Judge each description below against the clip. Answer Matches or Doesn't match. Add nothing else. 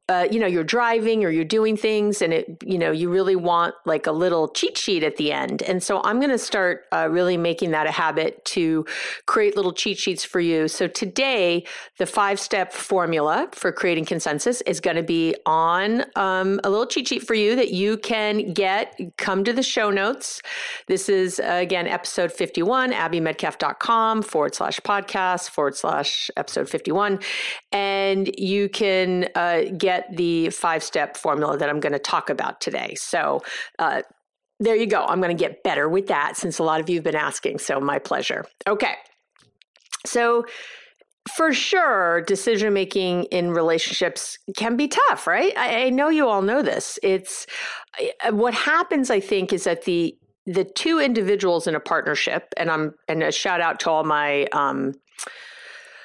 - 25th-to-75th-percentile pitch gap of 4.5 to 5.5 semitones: Matches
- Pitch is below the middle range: Doesn't match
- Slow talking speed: Doesn't match